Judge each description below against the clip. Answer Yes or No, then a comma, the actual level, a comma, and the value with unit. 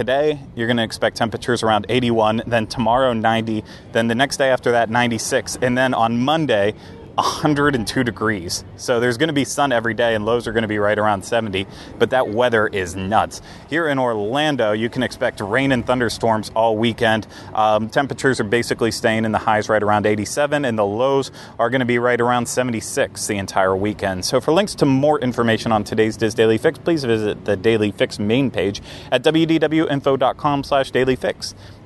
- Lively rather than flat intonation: No, average, 3.4 semitones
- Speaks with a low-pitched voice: Yes, low, 115 Hz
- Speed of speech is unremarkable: Yes, average, 195 wpm